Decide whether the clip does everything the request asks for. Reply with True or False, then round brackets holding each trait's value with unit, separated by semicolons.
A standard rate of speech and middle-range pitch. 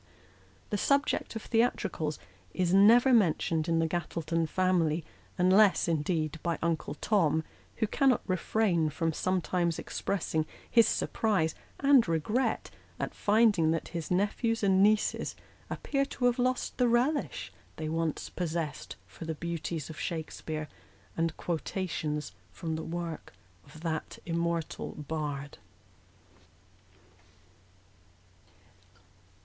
False (120 wpm; 170 Hz)